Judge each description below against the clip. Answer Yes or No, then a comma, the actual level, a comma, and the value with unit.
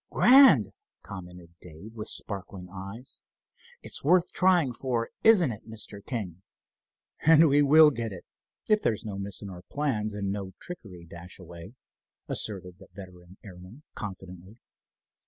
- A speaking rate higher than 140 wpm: No, slow, 135 wpm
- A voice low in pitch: Yes, low, 105 Hz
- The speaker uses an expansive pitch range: Yes, wide, 6.3 semitones